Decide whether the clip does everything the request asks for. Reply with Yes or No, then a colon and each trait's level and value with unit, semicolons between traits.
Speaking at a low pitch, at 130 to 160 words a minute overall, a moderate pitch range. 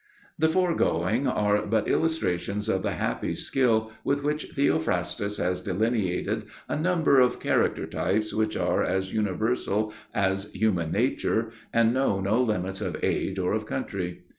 Yes: low, 110 Hz; average, 145 wpm; average, 4.5 semitones